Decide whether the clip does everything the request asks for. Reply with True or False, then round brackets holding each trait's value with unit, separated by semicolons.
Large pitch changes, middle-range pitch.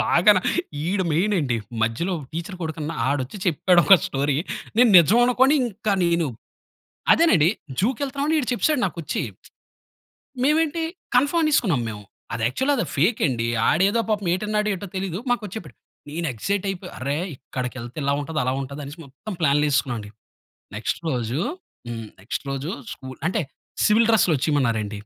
True (7.5 semitones; 170 Hz)